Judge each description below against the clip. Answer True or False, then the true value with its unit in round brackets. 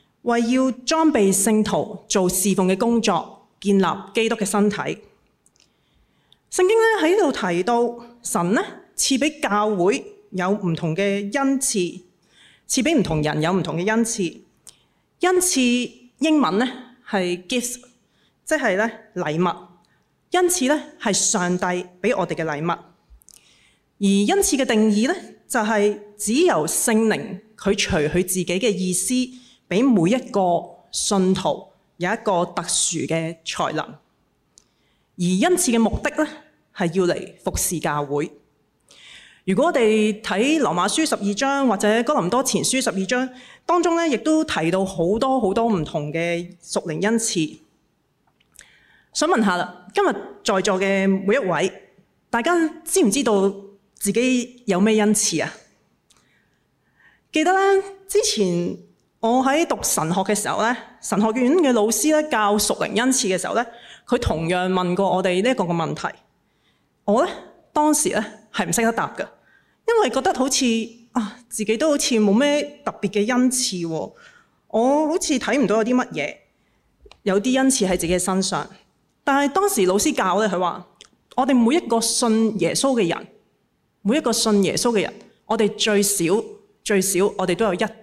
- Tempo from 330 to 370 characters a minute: False (220 characters per minute)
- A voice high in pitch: True (215 Hz)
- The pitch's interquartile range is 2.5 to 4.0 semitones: False (5.3 semitones)